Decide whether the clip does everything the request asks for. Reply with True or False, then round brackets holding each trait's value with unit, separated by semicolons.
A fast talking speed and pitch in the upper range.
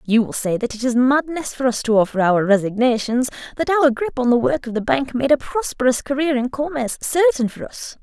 True (230 wpm; 255 Hz)